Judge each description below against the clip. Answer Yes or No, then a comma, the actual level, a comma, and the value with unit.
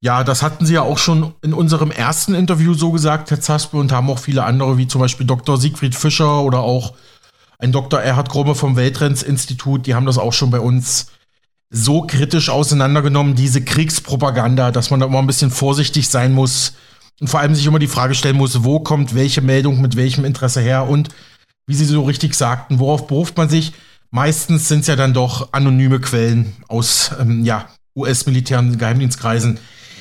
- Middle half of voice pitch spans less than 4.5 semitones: Yes, average, 2.8 semitones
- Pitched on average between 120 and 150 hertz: Yes, low, 135 Hz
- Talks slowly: No, fast, 190 wpm